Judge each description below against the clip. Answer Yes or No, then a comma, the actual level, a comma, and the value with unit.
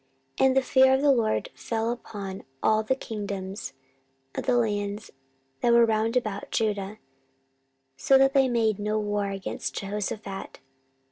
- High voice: Yes, high, 215 Hz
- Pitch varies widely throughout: No, average, 2.9 semitones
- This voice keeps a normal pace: Yes, average, 150 wpm